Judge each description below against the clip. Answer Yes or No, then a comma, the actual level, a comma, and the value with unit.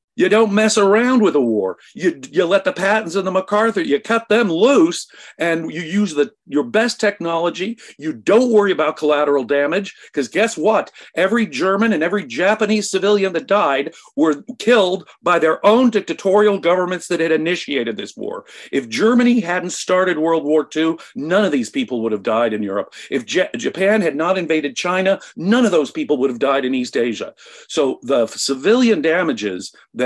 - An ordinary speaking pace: Yes, average, 185 wpm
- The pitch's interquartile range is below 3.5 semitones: No, average, 5.1 semitones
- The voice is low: No, high, 190 Hz